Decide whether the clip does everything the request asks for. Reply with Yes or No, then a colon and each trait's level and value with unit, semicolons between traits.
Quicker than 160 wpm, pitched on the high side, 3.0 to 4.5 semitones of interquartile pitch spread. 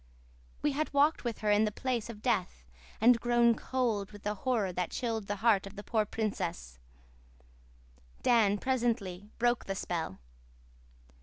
No: average, 155 wpm; high, 220 Hz; average, 3.4 semitones